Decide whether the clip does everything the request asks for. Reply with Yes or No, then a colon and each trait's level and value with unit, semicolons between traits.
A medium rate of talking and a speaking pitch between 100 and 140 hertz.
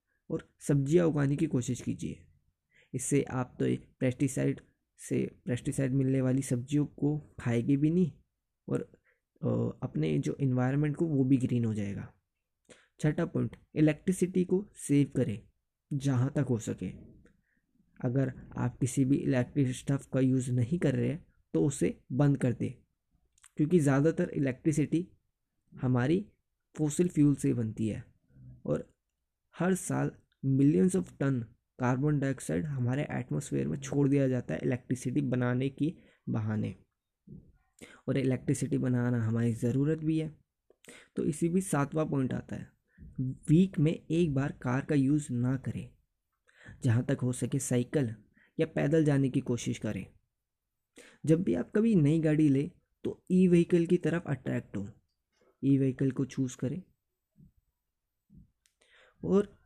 Yes: average, 140 wpm; low, 135 Hz